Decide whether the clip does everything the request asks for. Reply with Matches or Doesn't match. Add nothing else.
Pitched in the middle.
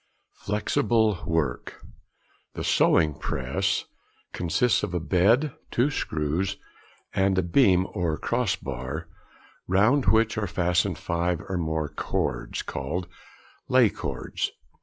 Doesn't match